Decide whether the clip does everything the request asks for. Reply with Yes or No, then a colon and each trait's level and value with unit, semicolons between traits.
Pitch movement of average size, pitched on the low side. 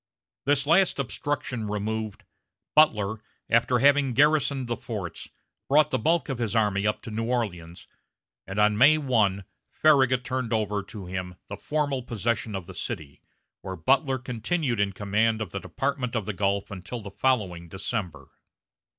Yes: average, 4.7 semitones; low, 110 Hz